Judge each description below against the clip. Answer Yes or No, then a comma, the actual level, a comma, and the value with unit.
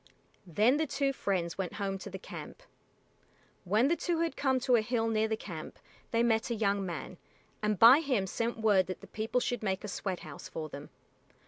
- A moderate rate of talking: No, fast, 210 wpm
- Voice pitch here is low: No, high, 215 Hz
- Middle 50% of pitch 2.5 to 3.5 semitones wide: No, average, 4.2 semitones